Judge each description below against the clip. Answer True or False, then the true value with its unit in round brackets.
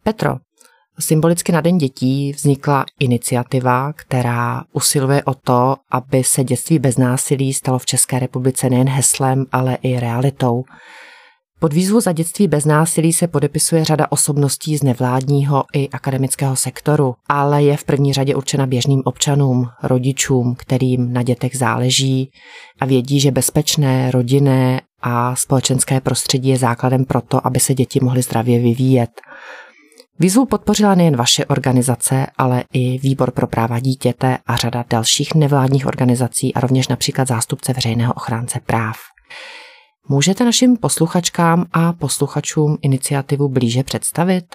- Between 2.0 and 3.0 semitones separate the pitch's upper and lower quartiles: True (2.6 semitones)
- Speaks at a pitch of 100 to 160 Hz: True (135 Hz)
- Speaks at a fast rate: False (135 wpm)